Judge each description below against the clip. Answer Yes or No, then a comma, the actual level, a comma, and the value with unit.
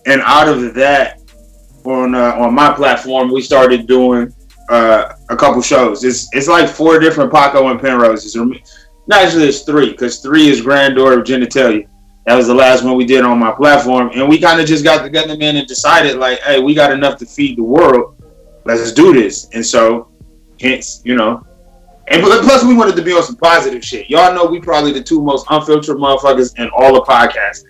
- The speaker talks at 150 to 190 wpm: No, average, 200 wpm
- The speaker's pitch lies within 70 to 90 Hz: No, low, 135 Hz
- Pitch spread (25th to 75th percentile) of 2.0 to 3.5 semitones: No, average, 3.9 semitones